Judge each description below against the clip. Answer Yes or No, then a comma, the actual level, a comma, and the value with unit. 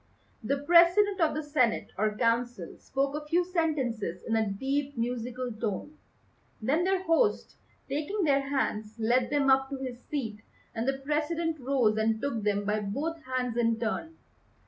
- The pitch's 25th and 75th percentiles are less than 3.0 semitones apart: No, average, 5.1 semitones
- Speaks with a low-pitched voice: No, very high, 265 Hz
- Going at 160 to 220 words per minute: Yes, average, 165 wpm